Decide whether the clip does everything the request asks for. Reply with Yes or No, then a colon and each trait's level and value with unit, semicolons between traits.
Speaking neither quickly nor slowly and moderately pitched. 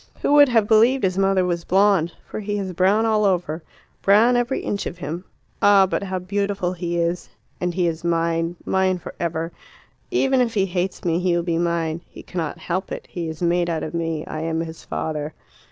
No: fast, 210 wpm; medium, 180 Hz